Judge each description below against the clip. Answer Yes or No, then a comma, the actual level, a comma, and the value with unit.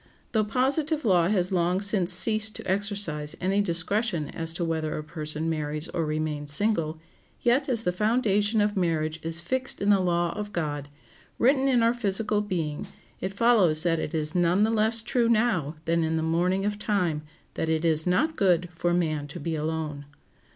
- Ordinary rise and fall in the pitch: Yes, average, 4.9 semitones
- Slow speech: No, average, 185 wpm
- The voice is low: No, medium, 180 Hz